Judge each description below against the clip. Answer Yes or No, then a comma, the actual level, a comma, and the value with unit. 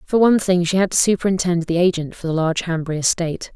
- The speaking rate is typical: No, fast, 235 wpm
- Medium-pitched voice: Yes, medium, 175 Hz